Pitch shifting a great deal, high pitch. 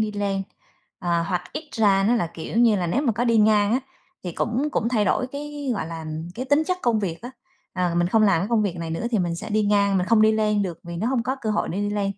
No: average, 4.4 semitones; high, 210 Hz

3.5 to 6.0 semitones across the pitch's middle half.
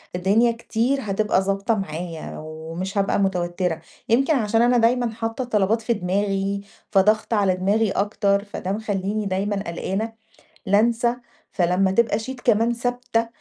No: average, 3.0 semitones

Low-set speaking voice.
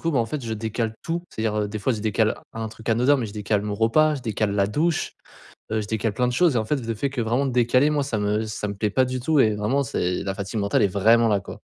Yes: low, 115 Hz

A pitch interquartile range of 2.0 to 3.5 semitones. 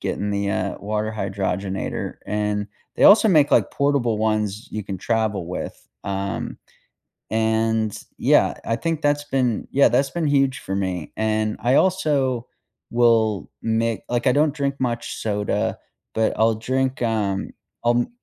No: average, 4.3 semitones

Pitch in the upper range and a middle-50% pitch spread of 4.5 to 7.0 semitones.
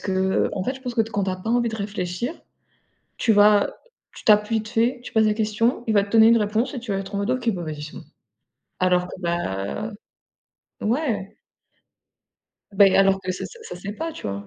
No: high, 210 Hz; average, 3.3 semitones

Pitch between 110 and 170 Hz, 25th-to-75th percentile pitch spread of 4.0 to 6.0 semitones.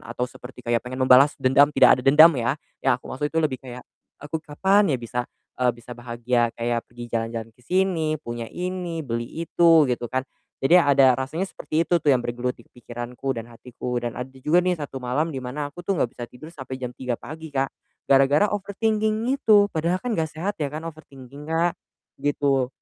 Yes: low, 135 Hz; average, 4.7 semitones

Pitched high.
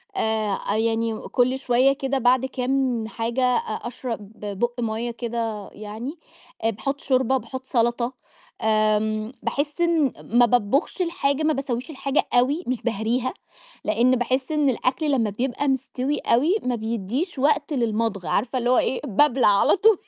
Yes: high, 245 Hz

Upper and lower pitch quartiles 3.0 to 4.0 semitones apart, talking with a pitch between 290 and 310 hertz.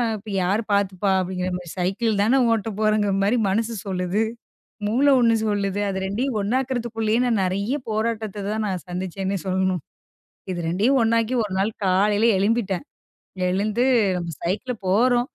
No: average, 3.3 semitones; high, 205 Hz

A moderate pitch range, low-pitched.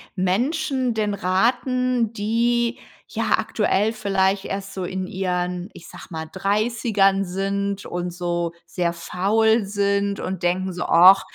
No: average, 3.3 semitones; high, 195 Hz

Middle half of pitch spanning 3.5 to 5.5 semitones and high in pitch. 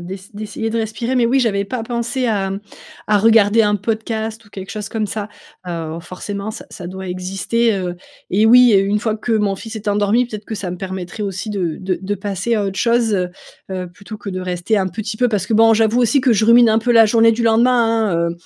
No: average, 2.8 semitones; high, 215 Hz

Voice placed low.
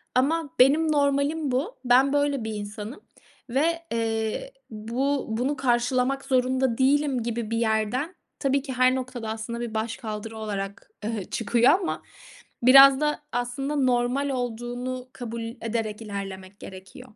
No: very high, 250 Hz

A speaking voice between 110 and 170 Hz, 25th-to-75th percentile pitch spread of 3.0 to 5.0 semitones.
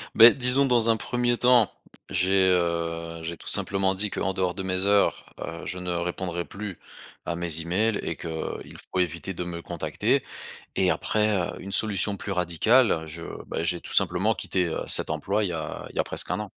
No: very low, 90 Hz; average, 3.6 semitones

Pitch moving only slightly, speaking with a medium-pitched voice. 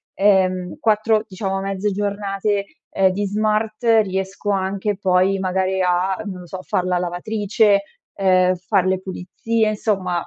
No: narrow, 1.9 semitones; high, 195 Hz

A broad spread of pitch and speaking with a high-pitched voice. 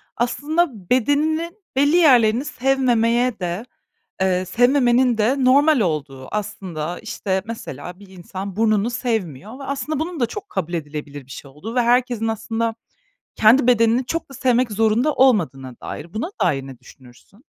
Yes: wide, 5.9 semitones; high, 225 Hz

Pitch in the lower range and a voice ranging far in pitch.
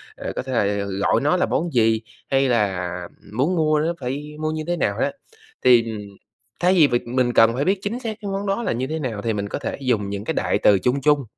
Yes: low, 130 Hz; wide, 6.0 semitones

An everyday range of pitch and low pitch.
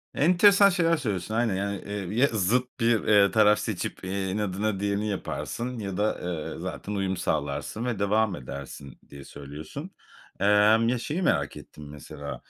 Yes: average, 3.8 semitones; low, 105 Hz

